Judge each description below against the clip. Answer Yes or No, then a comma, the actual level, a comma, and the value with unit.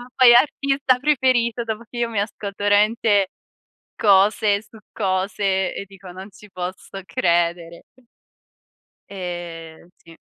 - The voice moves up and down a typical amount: Yes, average, 3.8 semitones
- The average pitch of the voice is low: No, high, 200 Hz